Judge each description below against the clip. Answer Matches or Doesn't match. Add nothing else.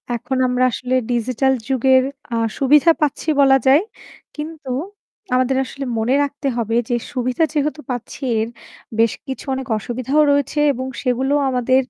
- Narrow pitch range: Matches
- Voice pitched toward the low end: Doesn't match